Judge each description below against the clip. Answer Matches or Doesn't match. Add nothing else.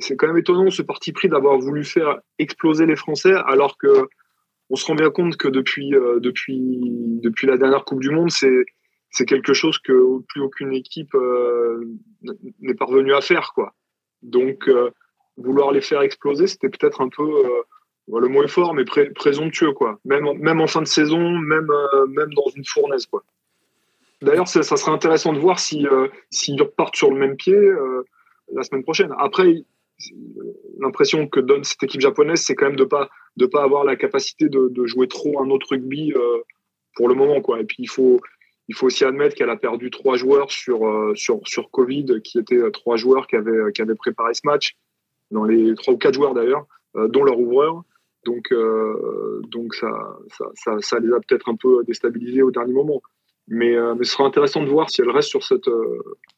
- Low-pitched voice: Doesn't match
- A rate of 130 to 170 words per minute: Doesn't match